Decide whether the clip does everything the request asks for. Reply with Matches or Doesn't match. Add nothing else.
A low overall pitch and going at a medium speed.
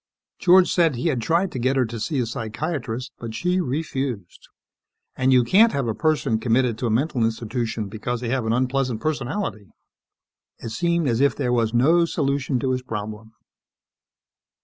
Matches